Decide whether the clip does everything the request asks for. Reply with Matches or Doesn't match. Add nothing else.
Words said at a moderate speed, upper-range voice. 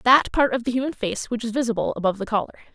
Doesn't match